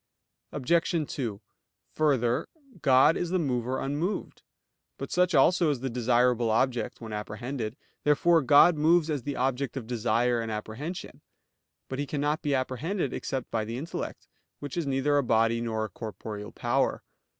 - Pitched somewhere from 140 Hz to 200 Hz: No, low, 130 Hz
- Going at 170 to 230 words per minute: No, average, 155 wpm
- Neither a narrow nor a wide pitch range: Yes, average, 4.2 semitones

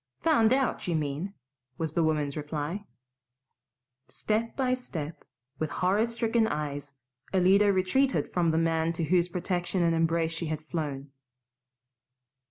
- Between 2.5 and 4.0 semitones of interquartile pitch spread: No, average, 4.5 semitones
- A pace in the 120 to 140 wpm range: Yes, slow, 135 wpm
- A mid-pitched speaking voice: Yes, medium, 170 Hz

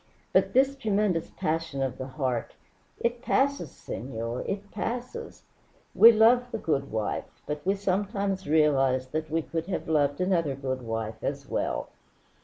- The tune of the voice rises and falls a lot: Yes, wide, 7.4 semitones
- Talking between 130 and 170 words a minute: Yes, average, 150 wpm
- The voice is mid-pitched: Yes, medium, 160 Hz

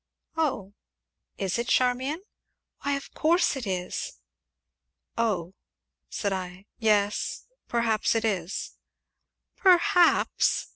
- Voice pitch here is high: Yes, high, 225 Hz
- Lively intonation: Yes, wide, 6.3 semitones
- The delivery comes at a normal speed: No, slow, 95 wpm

